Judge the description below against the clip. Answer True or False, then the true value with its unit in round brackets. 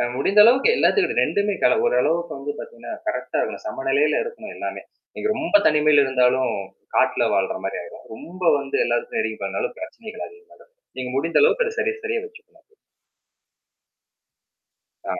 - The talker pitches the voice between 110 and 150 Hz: False (215 Hz)